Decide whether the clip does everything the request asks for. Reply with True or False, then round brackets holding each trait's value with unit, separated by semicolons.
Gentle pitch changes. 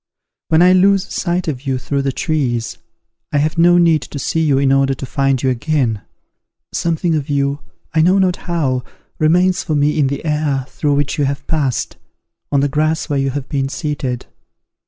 False (3.0 semitones)